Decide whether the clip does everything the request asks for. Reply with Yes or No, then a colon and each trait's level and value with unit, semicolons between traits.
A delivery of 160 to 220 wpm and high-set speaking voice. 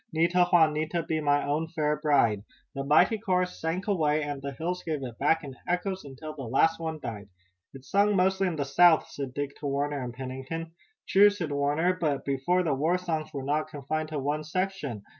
No: average, 200 wpm; medium, 155 Hz